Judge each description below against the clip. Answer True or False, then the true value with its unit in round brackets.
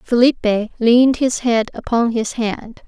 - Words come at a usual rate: True (145 wpm)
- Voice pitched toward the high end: True (235 Hz)